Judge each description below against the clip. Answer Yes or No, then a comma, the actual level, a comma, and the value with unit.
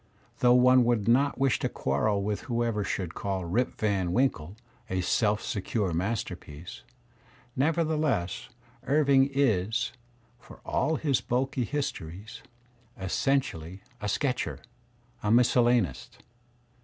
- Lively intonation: Yes, wide, 5.7 semitones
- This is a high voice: No, low, 115 Hz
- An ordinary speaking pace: No, slow, 115 wpm